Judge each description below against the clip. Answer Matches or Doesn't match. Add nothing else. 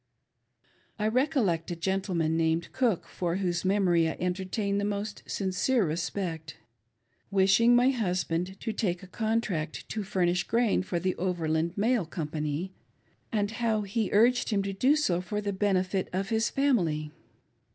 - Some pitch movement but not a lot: Matches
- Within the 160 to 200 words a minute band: Doesn't match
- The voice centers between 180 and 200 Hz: Matches